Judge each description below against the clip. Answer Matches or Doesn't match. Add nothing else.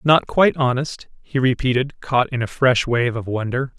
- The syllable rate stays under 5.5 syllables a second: Matches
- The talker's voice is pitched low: Matches